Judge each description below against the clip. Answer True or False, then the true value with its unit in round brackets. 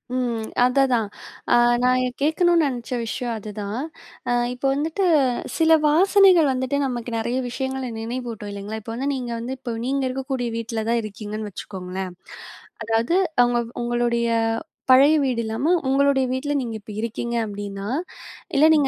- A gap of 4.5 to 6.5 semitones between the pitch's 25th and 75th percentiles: False (3.3 semitones)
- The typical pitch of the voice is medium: False (245 Hz)